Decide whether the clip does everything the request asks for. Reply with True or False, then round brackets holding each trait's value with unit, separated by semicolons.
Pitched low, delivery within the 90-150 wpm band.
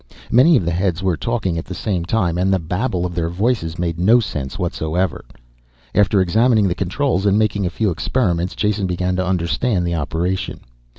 False (95 Hz; 190 wpm)